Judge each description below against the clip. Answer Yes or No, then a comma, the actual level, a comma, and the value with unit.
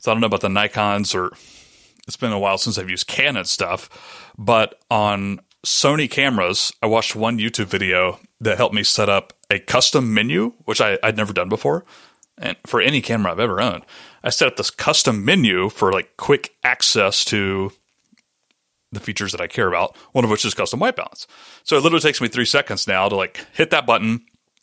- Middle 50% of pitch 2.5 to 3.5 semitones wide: Yes, average, 3.0 semitones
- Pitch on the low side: Yes, low, 110 Hz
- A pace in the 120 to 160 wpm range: No, fast, 205 wpm